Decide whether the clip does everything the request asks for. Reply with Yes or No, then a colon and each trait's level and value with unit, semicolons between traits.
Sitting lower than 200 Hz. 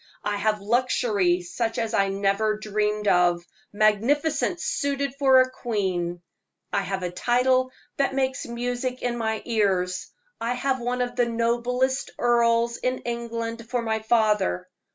No: high, 230 Hz